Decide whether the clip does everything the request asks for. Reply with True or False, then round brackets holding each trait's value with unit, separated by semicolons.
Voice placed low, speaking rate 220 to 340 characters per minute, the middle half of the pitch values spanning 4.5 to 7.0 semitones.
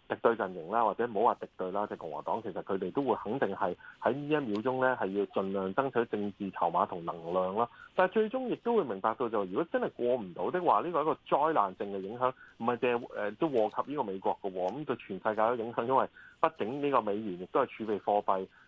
False (115 Hz; 365 characters per minute; 5.6 semitones)